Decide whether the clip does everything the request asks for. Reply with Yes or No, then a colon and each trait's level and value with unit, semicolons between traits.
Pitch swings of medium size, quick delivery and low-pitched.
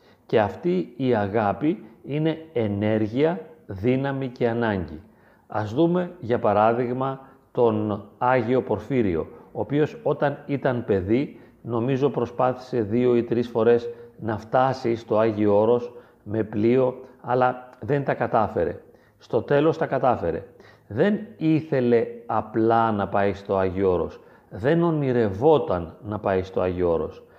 No: average, 3.7 semitones; average, 125 wpm; low, 120 Hz